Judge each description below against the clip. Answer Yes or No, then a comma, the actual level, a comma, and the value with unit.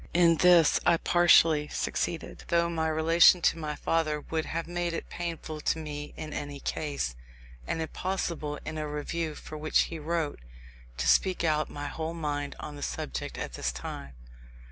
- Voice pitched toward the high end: No, medium, 160 Hz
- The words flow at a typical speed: Yes, average, 170 wpm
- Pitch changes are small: Yes, narrow, 2.1 semitones